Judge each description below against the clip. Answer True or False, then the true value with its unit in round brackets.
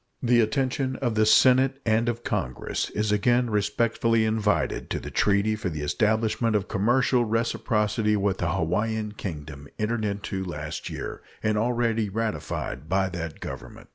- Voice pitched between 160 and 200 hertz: False (110 Hz)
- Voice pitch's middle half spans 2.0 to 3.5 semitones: True (2.7 semitones)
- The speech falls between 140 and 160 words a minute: True (150 wpm)